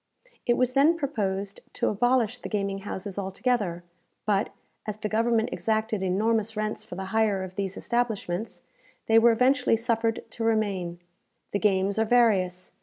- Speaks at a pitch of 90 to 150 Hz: No, high, 215 Hz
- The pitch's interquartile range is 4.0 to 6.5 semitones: No, average, 2.9 semitones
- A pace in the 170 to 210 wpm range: No, average, 155 wpm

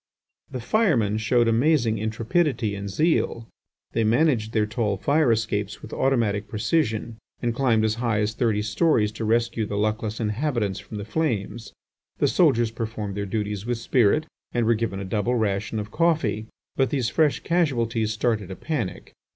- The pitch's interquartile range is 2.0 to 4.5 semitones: Yes, average, 2.7 semitones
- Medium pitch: No, low, 115 Hz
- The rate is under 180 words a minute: Yes, average, 165 wpm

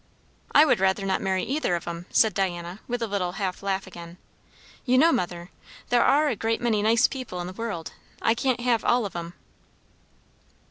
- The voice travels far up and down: No, average, 5.0 semitones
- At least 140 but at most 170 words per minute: No, average, 195 wpm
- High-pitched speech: Yes, high, 200 Hz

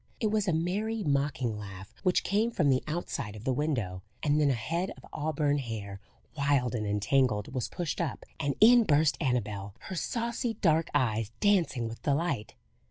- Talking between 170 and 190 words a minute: Yes, average, 175 wpm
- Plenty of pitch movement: Yes, wide, 7.3 semitones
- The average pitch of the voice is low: No, medium, 145 Hz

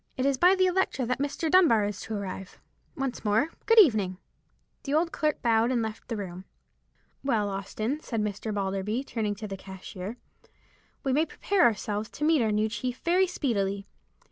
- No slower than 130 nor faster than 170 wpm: No, average, 180 wpm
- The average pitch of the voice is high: Yes, high, 225 Hz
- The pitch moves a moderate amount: No, wide, 5.8 semitones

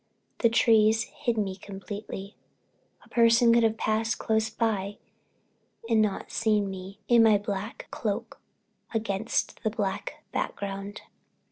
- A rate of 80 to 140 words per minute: Yes, slow, 135 wpm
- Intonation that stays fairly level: Yes, narrow, 2.2 semitones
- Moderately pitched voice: No, high, 215 Hz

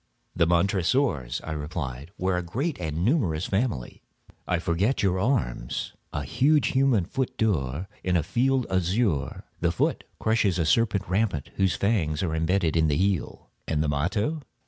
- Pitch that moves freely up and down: Yes, wide, 5.8 semitones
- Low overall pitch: Yes, very low, 90 Hz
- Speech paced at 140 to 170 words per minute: Yes, average, 160 wpm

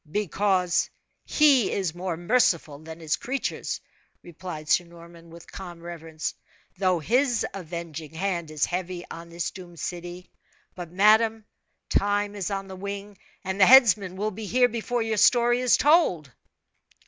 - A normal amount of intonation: Yes, average, 3.9 semitones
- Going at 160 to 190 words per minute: No, average, 150 wpm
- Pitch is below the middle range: No, medium, 185 Hz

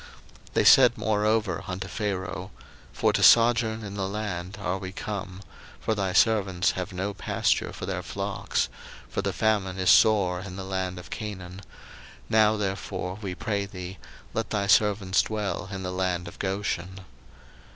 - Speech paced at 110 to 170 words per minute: Yes, average, 160 wpm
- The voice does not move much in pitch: Yes, narrow, 2.3 semitones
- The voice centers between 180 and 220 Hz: No, very low, 95 Hz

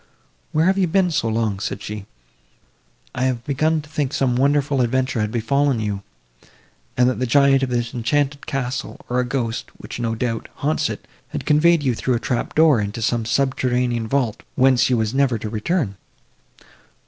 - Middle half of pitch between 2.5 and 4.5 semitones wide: Yes, average, 3.3 semitones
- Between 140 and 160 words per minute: No, average, 185 wpm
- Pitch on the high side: No, low, 125 Hz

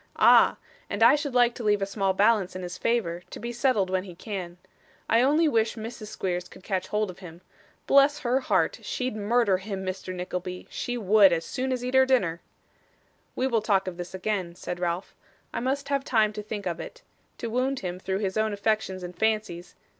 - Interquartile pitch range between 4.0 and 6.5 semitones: Yes, average, 4.5 semitones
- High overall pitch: Yes, high, 210 Hz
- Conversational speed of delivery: No, fast, 210 wpm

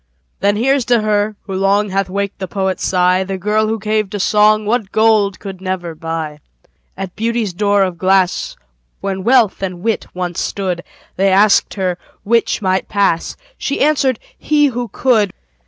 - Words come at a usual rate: Yes, average, 170 wpm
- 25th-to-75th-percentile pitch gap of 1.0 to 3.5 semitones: Yes, narrow, 2.5 semitones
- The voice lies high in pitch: Yes, high, 200 Hz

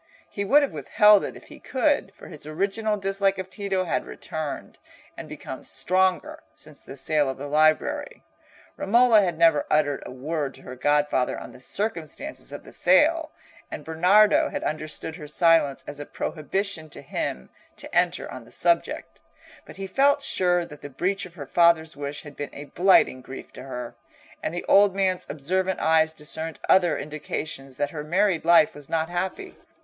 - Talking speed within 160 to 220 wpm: Yes, average, 180 wpm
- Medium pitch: Yes, medium, 165 Hz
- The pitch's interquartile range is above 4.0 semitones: Yes, average, 4.8 semitones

